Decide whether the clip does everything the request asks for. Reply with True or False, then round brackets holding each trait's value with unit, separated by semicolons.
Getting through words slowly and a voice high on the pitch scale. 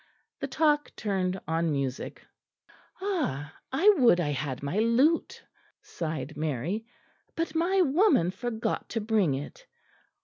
True (125 wpm; 200 Hz)